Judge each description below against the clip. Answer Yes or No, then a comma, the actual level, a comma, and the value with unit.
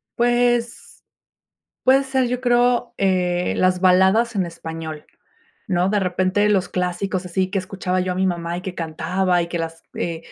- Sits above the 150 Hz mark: Yes, medium, 185 Hz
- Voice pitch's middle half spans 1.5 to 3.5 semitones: No, average, 4.1 semitones